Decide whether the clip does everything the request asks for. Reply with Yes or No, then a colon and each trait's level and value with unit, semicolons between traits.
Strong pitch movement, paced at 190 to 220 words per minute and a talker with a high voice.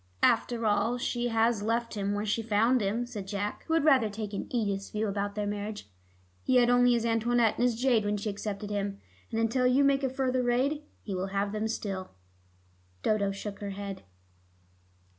No: average, 3.1 semitones; average, 195 wpm; high, 220 Hz